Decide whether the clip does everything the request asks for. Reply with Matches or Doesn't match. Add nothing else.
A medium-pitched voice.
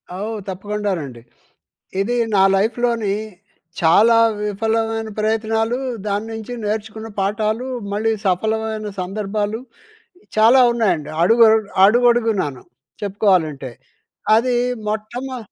Doesn't match